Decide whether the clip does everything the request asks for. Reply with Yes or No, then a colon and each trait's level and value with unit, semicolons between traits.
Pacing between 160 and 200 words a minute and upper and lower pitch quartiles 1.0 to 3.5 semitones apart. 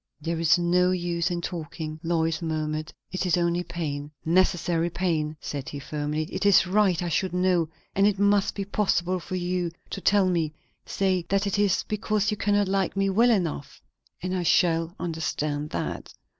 Yes: average, 180 wpm; average, 2.9 semitones